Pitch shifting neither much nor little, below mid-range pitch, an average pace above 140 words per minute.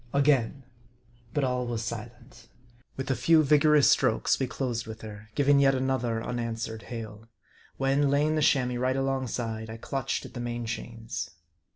Yes: average, 3.0 semitones; low, 125 Hz; average, 165 wpm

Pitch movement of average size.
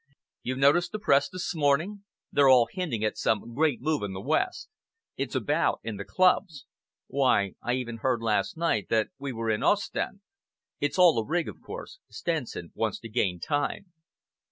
No: wide, 7.1 semitones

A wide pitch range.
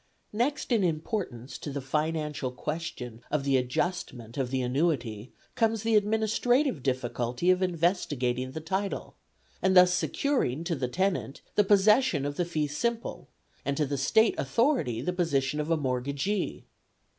Yes: wide, 6.9 semitones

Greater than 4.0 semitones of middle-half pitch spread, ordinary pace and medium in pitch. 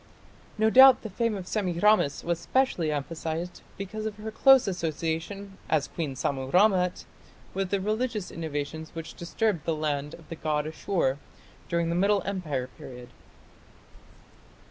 Yes: average, 4.8 semitones; average, 145 wpm; medium, 175 Hz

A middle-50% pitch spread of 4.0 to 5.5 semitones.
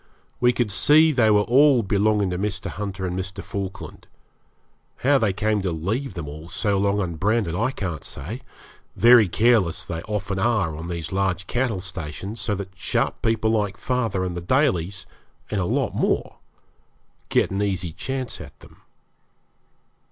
No: average, 3.5 semitones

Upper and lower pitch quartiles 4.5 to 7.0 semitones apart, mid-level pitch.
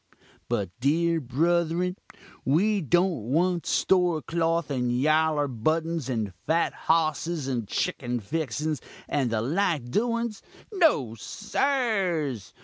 Yes: average, 5.1 semitones; medium, 160 Hz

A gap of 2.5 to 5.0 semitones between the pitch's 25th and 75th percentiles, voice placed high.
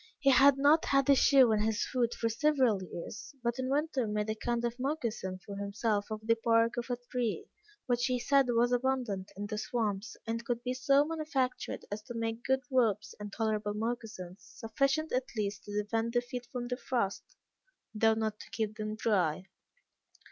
Yes: average, 3.2 semitones; high, 230 Hz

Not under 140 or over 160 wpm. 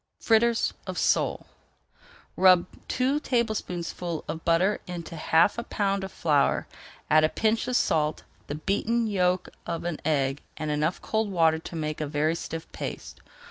Yes: average, 155 wpm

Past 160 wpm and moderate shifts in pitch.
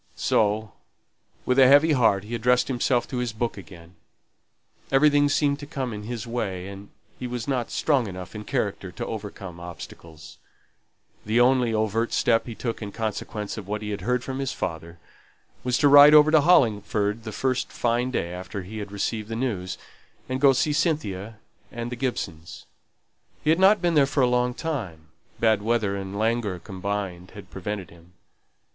Yes: average, 180 wpm; average, 4.5 semitones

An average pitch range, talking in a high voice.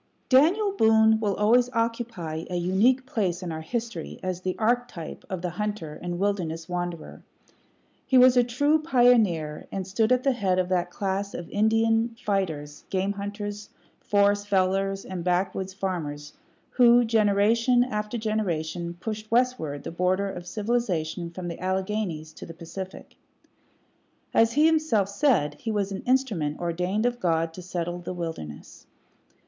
Yes: average, 4.5 semitones; high, 200 Hz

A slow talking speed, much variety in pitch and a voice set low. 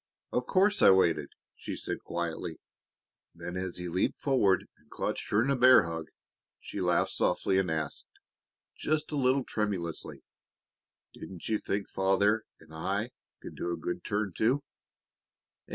No: average, 150 wpm; wide, 5.8 semitones; very low, 95 Hz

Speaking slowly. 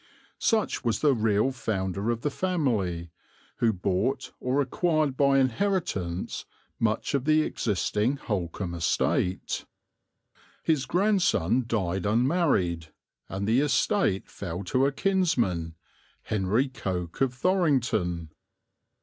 Yes: slow, 110 wpm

